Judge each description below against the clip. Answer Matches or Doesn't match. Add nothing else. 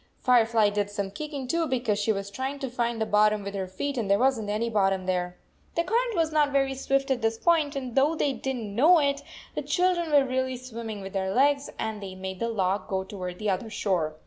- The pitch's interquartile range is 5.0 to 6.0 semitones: Matches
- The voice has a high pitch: Matches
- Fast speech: Matches